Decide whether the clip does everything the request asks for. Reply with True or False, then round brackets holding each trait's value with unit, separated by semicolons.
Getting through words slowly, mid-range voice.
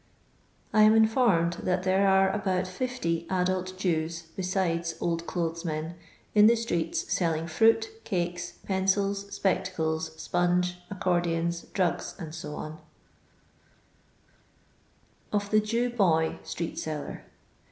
True (110 wpm; 180 Hz)